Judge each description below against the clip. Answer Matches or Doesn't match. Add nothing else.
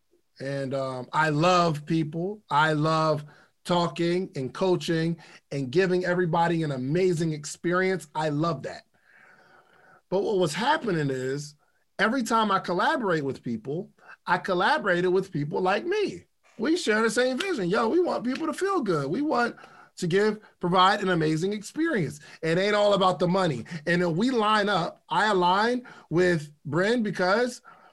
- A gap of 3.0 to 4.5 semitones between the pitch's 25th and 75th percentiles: Doesn't match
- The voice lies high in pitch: Doesn't match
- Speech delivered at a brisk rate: Doesn't match